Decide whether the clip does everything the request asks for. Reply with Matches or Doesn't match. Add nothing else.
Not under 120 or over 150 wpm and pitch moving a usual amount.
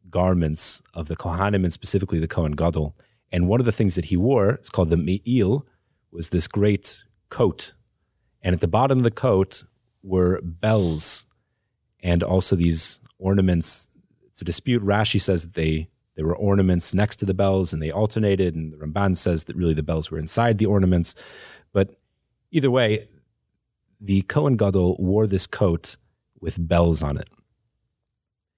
Doesn't match